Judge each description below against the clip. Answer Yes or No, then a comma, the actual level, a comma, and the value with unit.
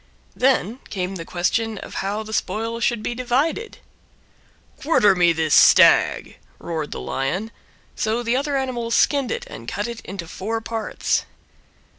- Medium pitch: No, high, 220 Hz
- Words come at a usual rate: Yes, average, 145 wpm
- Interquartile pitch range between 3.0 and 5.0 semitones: Yes, average, 4.7 semitones